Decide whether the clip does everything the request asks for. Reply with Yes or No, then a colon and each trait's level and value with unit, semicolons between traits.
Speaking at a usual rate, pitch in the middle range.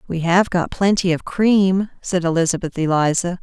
Yes: average, 160 wpm; medium, 180 Hz